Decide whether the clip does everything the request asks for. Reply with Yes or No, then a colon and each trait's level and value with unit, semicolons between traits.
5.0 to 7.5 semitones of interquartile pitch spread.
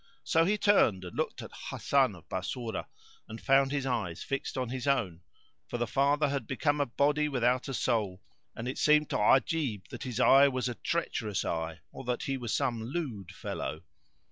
No: average, 4.0 semitones